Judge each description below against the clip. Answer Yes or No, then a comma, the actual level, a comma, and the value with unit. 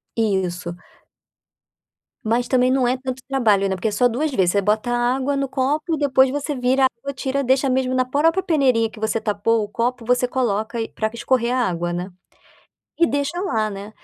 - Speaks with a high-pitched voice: Yes, very high, 250 Hz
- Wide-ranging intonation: No, average, 3.7 semitones